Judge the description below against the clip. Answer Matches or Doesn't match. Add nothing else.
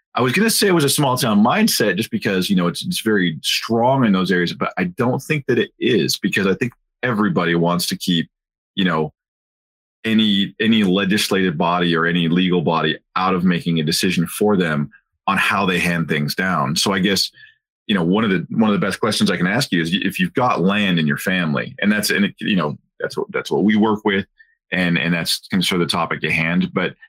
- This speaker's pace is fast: Matches